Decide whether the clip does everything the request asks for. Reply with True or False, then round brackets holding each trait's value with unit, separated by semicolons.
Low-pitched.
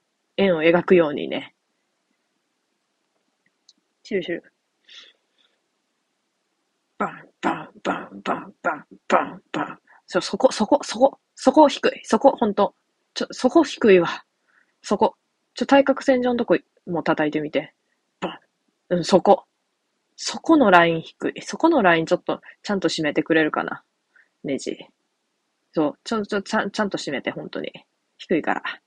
False (205 Hz)